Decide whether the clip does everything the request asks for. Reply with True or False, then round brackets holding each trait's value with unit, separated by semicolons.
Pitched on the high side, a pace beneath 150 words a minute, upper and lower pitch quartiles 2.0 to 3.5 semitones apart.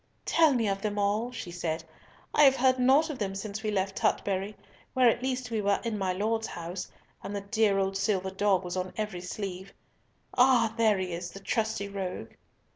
False (205 Hz; 200 wpm; 3.1 semitones)